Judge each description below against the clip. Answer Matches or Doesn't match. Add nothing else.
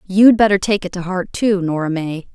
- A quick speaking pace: Matches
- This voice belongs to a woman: Matches